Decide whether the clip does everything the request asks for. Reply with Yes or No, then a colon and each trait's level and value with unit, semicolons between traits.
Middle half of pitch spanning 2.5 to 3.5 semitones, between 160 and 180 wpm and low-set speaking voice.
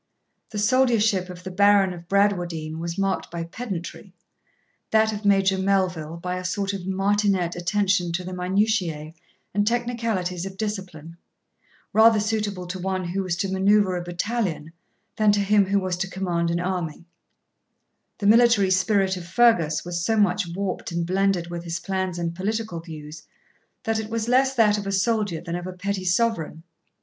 No: average, 2.9 semitones; average, 170 wpm; high, 190 Hz